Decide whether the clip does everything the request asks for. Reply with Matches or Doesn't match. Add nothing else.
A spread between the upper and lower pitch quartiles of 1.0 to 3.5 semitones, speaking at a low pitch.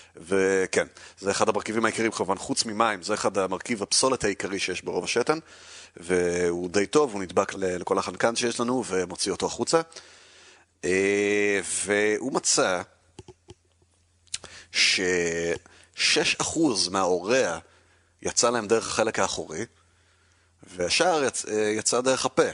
Doesn't match